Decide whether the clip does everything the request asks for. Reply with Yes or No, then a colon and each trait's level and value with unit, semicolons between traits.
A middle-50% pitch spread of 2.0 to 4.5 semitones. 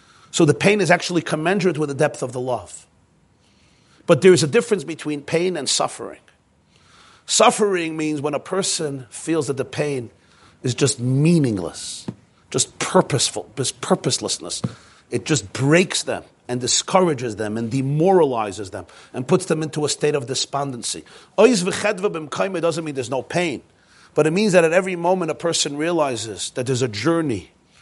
No: average, 5.0 semitones